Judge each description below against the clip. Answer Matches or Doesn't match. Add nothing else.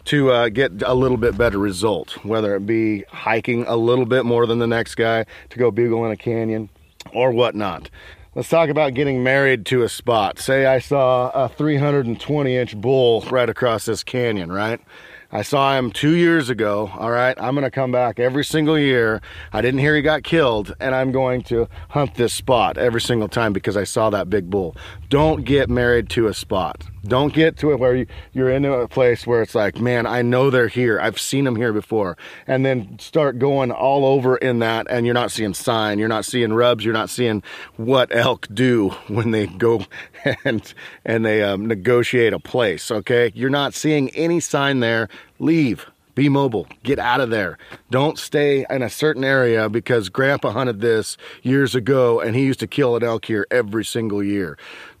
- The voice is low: Matches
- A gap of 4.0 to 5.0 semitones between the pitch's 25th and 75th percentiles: Doesn't match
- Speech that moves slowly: Doesn't match